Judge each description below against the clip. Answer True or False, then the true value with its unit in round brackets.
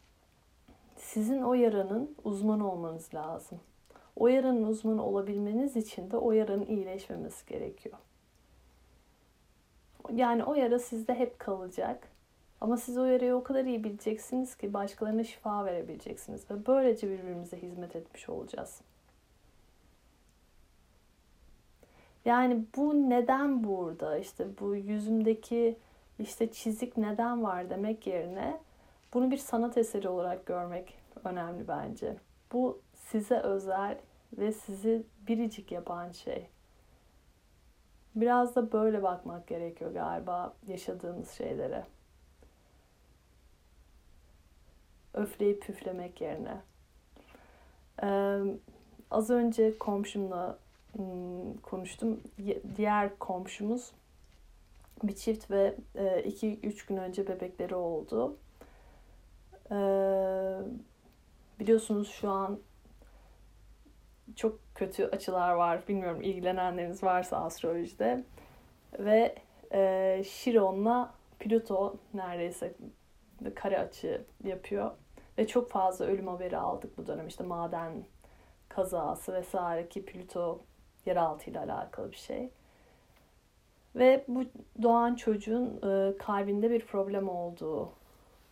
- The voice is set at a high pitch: True (200 Hz)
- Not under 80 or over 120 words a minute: True (100 wpm)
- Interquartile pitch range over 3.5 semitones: True (4.4 semitones)